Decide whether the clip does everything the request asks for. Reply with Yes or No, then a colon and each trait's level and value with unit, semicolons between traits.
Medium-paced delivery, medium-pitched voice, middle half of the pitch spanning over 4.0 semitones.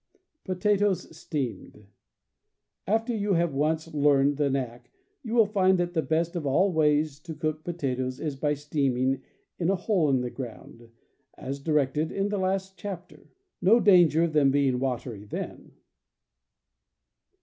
Yes: average, 150 wpm; medium, 155 Hz; average, 5.3 semitones